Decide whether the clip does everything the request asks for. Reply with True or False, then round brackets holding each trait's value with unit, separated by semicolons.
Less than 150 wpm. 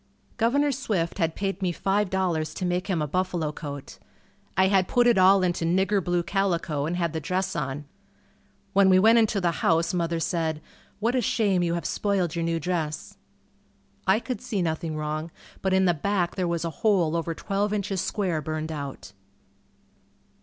False (180 wpm)